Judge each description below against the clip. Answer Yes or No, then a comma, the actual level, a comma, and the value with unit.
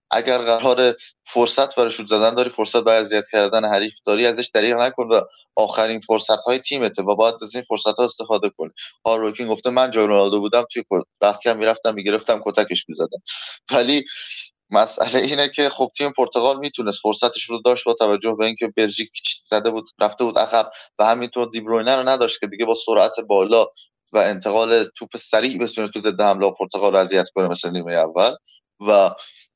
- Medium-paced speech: No, fast, 185 wpm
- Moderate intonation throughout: No, narrow, 2.3 semitones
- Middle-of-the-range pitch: No, low, 115 Hz